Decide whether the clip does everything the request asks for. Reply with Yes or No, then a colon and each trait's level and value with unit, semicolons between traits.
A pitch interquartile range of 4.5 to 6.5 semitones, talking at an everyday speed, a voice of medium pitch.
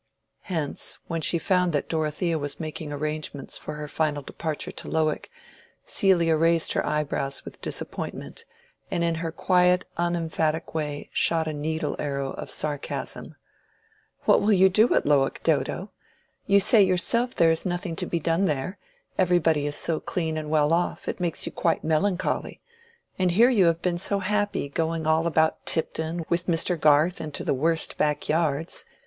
No: average, 2.7 semitones; average, 165 wpm; medium, 165 Hz